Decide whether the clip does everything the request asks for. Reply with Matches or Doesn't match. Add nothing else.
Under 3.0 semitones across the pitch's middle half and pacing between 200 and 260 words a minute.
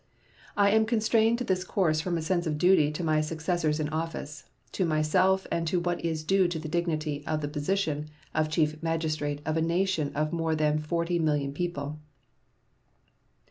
Doesn't match